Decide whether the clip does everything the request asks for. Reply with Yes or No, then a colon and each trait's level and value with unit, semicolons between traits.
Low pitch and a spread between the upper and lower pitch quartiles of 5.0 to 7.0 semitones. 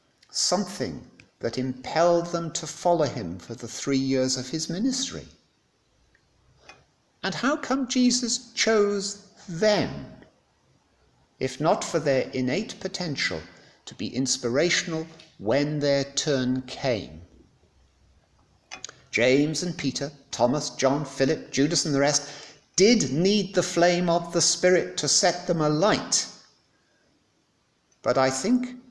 No: medium, 155 Hz; wide, 5.6 semitones